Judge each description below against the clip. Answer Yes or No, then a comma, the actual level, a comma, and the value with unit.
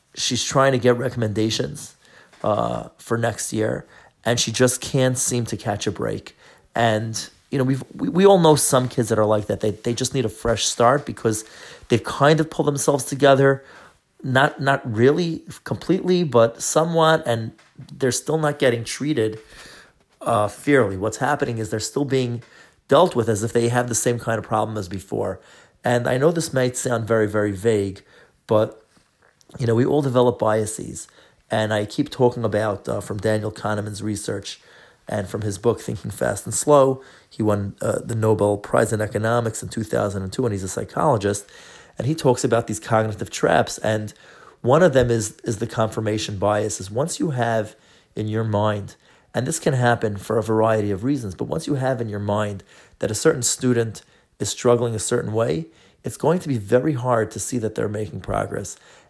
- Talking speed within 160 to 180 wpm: No, average, 195 wpm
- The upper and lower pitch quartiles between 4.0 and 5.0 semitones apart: No, average, 3.5 semitones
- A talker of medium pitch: No, low, 115 Hz